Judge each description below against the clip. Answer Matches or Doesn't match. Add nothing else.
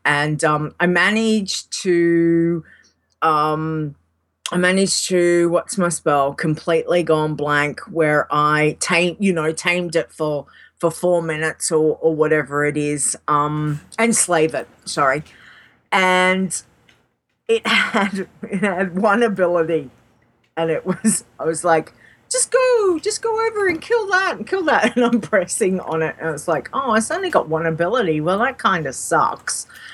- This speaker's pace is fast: Doesn't match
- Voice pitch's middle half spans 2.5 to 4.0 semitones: Doesn't match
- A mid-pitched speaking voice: Matches